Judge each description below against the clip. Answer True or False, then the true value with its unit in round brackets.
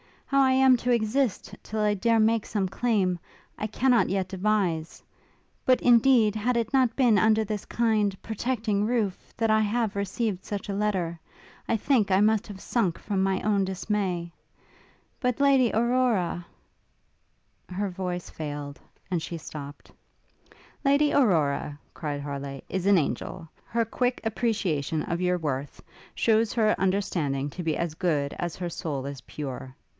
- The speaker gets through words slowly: False (155 wpm)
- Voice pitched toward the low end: False (200 Hz)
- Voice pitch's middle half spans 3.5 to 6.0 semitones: True (4.9 semitones)